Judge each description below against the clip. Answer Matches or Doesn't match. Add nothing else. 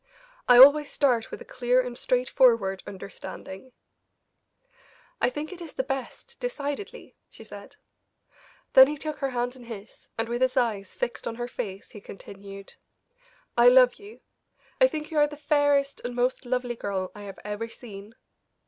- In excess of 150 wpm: Matches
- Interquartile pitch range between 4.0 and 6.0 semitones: Matches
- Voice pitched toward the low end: Doesn't match